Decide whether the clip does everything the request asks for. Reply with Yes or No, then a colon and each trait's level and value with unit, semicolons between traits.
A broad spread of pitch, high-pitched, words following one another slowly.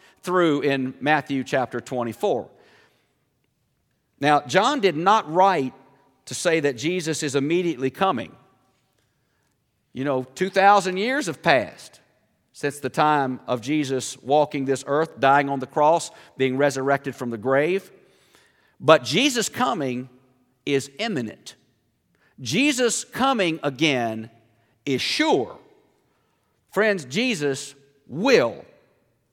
No: wide, 5.9 semitones; medium, 145 Hz; slow, 110 wpm